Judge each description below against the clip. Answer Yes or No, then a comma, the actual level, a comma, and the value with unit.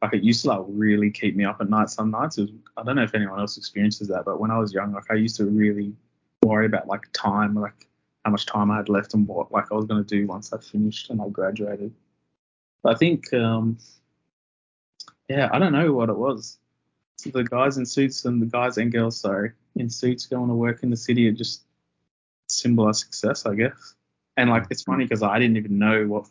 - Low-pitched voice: Yes, low, 110 Hz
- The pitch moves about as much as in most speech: No, narrow, 2.1 semitones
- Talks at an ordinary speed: No, fast, 240 wpm